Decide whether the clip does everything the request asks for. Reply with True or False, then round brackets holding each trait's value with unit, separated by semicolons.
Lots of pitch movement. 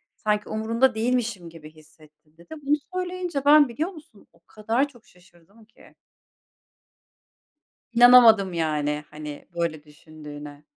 True (8.1 semitones)